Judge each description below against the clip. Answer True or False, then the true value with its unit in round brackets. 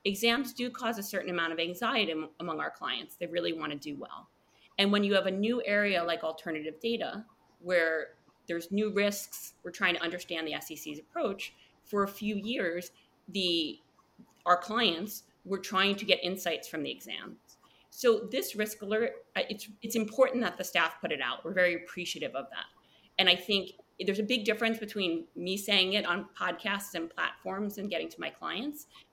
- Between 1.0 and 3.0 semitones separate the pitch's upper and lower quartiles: False (3.9 semitones)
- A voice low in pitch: False (195 Hz)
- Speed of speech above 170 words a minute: True (185 wpm)